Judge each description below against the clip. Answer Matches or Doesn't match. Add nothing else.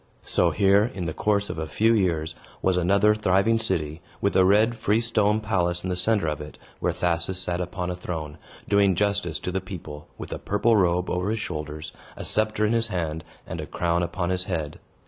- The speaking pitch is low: Matches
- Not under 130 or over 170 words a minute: Doesn't match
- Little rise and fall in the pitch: Doesn't match